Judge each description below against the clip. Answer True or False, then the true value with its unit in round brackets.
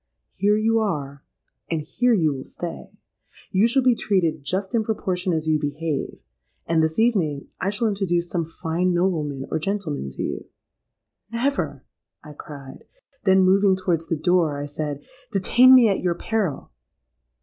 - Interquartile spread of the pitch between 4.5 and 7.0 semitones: True (4.8 semitones)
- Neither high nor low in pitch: True (175 Hz)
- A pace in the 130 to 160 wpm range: True (155 wpm)